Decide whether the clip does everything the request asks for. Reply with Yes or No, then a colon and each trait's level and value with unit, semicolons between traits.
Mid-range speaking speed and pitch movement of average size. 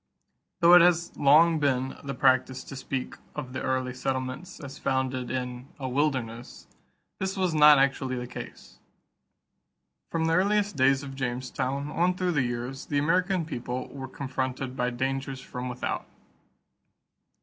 Yes: average, 150 wpm; average, 3.1 semitones